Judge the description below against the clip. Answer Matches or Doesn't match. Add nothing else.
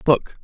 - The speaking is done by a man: Matches